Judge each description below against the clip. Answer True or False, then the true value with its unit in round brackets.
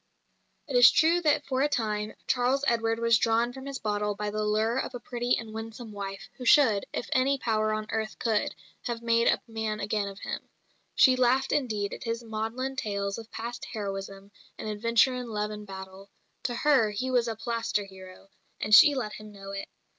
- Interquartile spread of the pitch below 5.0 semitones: True (2.9 semitones)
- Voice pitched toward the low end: False (225 Hz)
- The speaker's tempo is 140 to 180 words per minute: False (200 wpm)